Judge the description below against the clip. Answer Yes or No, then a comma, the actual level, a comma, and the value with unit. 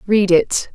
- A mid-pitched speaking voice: No, high, 195 Hz